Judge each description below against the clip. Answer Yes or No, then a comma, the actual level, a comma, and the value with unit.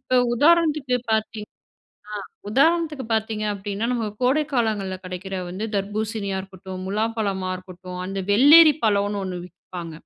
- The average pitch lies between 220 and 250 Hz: No, high, 210 Hz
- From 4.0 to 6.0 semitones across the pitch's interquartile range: Yes, average, 4.6 semitones